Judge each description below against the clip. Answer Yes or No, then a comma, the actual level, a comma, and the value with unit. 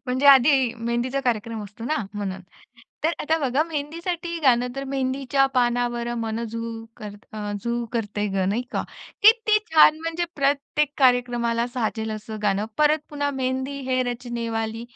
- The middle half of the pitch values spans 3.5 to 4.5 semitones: Yes, average, 3.8 semitones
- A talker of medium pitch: No, high, 245 Hz